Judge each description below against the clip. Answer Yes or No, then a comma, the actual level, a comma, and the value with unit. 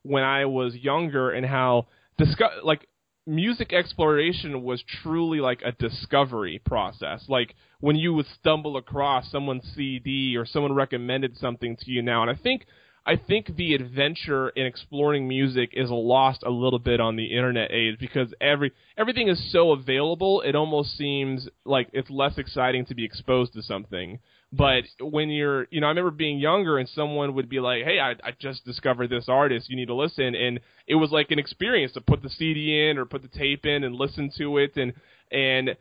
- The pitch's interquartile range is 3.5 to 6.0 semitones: No, average, 2.8 semitones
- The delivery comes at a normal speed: Yes, average, 195 wpm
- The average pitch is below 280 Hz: Yes, low, 135 Hz